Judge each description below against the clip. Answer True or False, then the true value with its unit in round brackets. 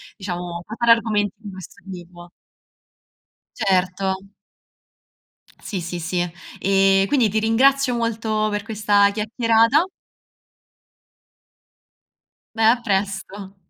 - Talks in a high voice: True (205 Hz)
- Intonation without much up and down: False (3.1 semitones)